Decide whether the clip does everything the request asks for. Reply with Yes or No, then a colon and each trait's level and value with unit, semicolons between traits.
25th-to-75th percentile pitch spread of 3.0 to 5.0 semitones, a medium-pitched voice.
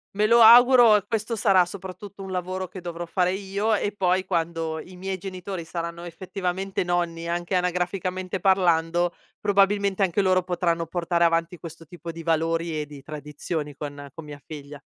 No: narrow, 2.6 semitones; medium, 180 Hz